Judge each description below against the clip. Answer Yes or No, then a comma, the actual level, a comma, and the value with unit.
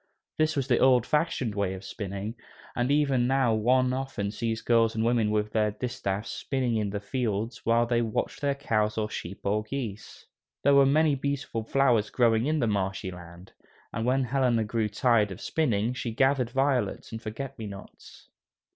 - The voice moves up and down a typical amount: Yes, average, 3.8 semitones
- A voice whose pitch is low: Yes, low, 115 Hz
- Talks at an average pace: Yes, average, 180 wpm